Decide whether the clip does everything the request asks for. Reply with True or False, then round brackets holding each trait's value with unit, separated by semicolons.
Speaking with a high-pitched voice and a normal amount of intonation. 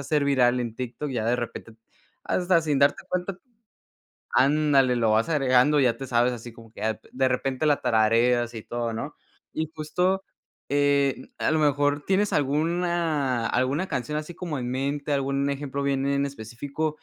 False (140 Hz; 3.5 semitones)